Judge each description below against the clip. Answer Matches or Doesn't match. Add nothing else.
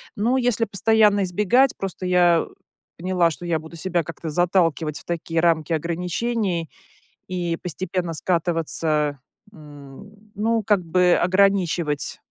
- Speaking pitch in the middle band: Matches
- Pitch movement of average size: Matches